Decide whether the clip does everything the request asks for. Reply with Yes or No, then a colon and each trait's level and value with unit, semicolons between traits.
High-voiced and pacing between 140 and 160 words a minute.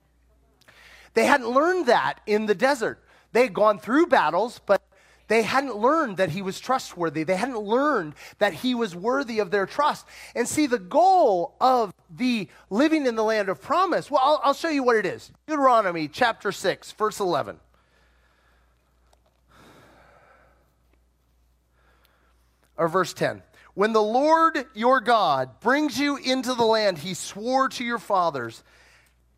Yes: high, 210 Hz; average, 150 wpm